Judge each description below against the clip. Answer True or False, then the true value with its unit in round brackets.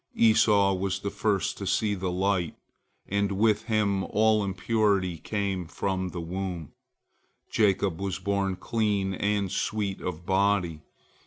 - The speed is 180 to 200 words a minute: False (135 wpm)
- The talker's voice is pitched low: True (100 Hz)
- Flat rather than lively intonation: True (1.7 semitones)